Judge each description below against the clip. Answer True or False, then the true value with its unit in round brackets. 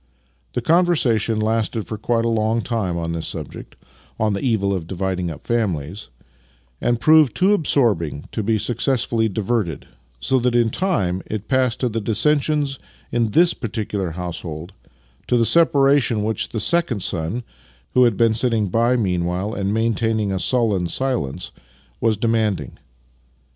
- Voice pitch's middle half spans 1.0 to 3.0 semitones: False (4.3 semitones)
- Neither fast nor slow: True (160 wpm)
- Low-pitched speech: True (110 Hz)